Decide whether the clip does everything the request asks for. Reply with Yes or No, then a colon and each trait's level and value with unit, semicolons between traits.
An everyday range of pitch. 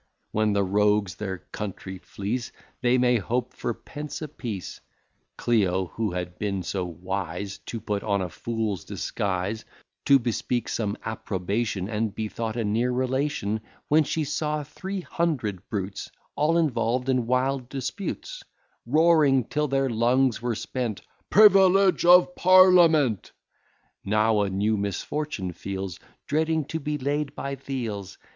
No: wide, 6.1 semitones